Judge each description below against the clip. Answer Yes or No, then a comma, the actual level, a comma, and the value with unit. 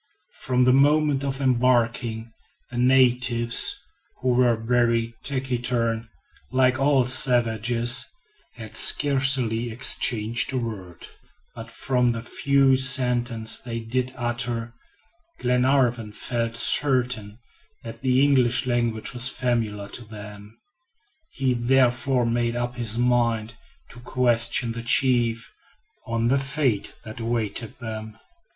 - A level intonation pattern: Yes, narrow, 1.8 semitones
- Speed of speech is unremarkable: No, slow, 115 wpm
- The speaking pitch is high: No, low, 120 Hz